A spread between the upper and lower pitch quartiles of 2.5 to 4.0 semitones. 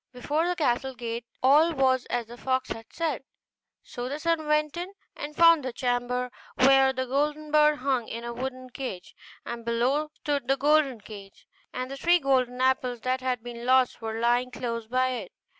Yes: average, 3.2 semitones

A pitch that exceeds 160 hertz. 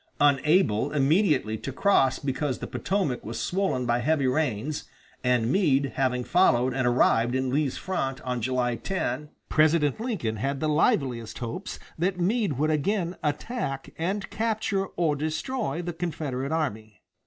No: medium, 145 Hz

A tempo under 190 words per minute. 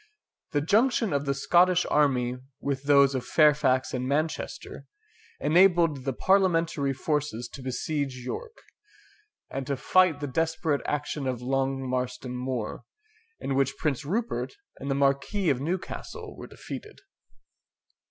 Yes: slow, 135 wpm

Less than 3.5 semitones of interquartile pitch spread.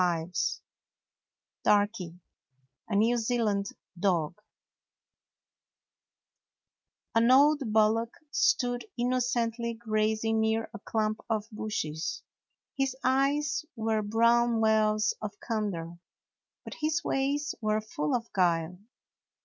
Yes: narrow, 2.6 semitones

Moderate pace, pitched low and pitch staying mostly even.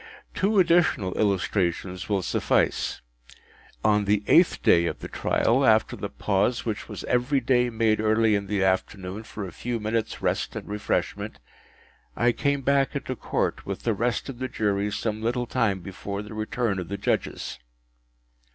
No: average, 165 wpm; low, 110 Hz; average, 3.4 semitones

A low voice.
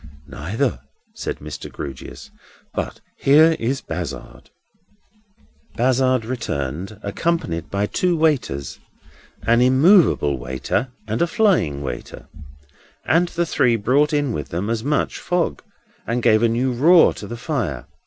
Yes: low, 120 Hz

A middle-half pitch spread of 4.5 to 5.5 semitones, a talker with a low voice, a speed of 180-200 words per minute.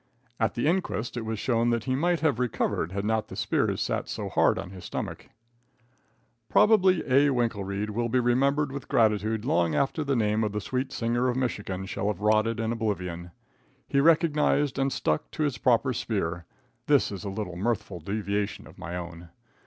Yes: average, 4.8 semitones; low, 115 Hz; average, 185 wpm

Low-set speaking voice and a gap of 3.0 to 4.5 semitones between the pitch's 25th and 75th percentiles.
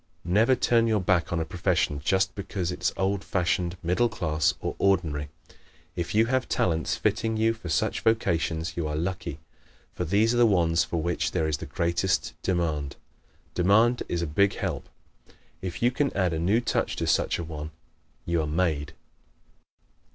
Yes: very low, 90 Hz; average, 4.1 semitones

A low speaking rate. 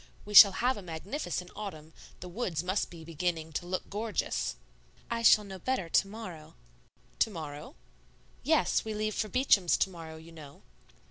No: average, 165 wpm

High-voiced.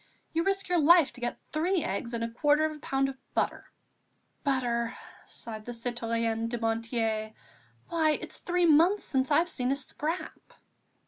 Yes: very high, 265 Hz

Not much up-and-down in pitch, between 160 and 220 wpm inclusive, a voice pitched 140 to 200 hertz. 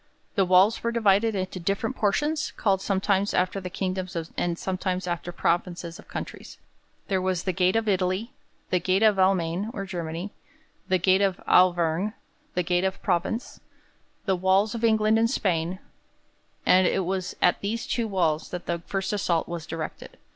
Yes: narrow, 2.2 semitones; average, 170 wpm; high, 190 Hz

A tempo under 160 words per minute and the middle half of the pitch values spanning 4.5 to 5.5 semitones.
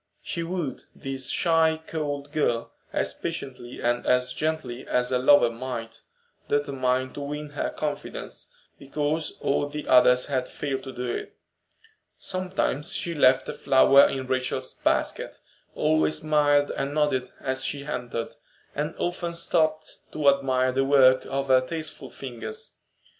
No: average, 140 wpm; average, 2.9 semitones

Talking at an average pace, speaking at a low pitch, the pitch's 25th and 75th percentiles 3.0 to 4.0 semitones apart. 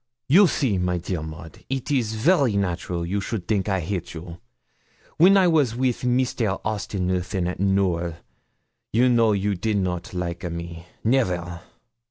No: average, 165 wpm; very low, 95 Hz; average, 5.3 semitones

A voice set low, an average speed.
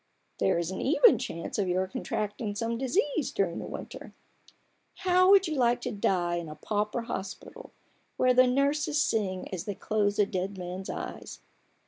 No: high, 210 Hz; average, 170 wpm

